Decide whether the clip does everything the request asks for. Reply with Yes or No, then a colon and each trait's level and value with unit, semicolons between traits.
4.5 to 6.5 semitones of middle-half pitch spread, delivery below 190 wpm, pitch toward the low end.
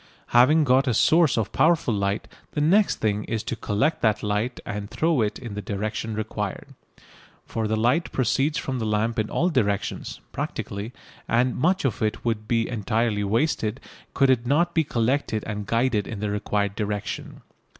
No: average, 4.1 semitones; average, 175 wpm; low, 115 Hz